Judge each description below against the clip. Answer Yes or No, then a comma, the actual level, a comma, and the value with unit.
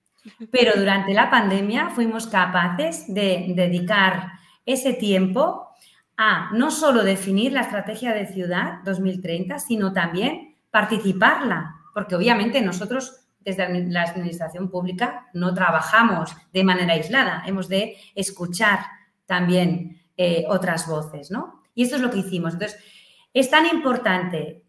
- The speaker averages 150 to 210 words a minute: No, slow, 125 wpm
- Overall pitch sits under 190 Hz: No, high, 195 Hz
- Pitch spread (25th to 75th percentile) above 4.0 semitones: Yes, average, 4.4 semitones